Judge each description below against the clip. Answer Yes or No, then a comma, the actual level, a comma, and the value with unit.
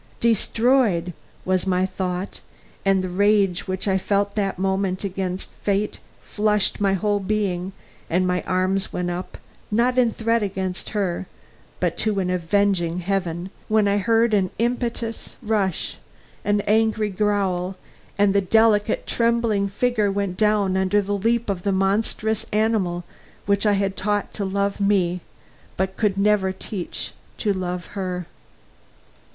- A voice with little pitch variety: Yes, narrow, 2.2 semitones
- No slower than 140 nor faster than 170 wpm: Yes, average, 145 wpm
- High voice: Yes, high, 200 Hz